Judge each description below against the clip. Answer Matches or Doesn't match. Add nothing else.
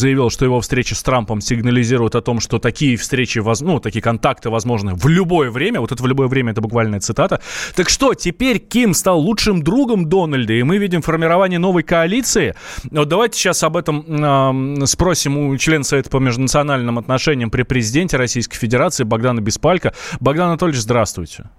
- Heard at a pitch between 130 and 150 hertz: Matches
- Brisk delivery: Matches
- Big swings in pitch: Matches